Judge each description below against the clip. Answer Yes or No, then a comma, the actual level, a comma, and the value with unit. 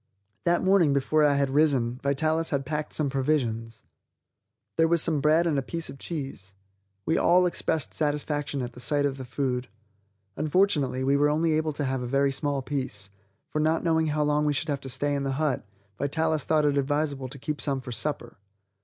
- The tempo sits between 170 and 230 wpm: Yes, average, 200 wpm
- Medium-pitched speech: Yes, medium, 145 Hz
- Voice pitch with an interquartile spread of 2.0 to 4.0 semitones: Yes, narrow, 2.6 semitones